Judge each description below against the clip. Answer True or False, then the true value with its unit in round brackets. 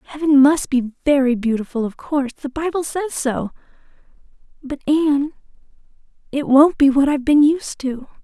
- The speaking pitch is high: True (280 Hz)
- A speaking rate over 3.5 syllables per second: True (5.0 syllables/s)